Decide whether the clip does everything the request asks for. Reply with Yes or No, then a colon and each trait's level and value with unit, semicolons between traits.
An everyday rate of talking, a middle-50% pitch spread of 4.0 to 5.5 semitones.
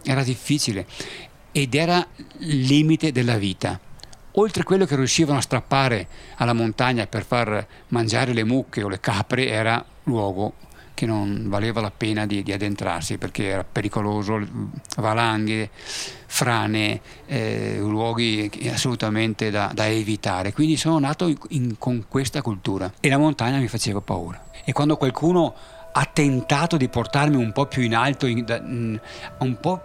Yes: average, 150 wpm; average, 4.4 semitones